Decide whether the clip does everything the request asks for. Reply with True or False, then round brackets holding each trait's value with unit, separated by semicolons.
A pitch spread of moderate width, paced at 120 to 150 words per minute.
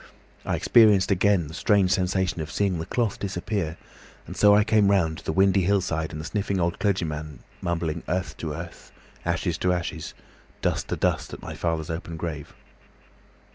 False (3.5 semitones; 175 wpm)